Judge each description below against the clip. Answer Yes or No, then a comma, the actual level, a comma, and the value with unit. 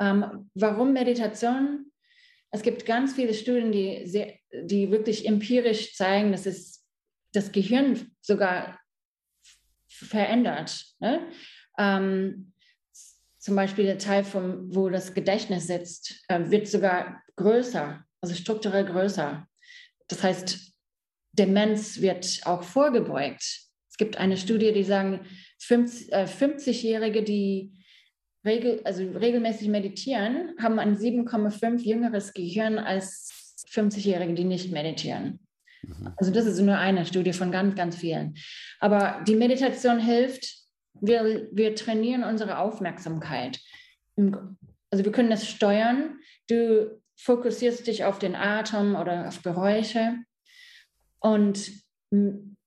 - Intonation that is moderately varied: Yes, average, 3.4 semitones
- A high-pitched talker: Yes, high, 210 Hz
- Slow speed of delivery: Yes, slow, 115 wpm